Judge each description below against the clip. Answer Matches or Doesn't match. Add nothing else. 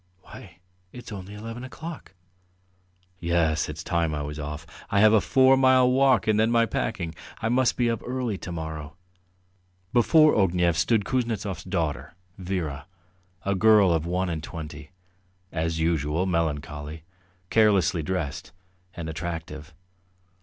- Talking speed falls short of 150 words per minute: Matches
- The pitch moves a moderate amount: Doesn't match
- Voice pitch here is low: Matches